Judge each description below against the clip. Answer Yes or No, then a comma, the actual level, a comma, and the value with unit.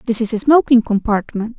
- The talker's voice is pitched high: Yes, high, 230 Hz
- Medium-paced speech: Yes, average, 190 wpm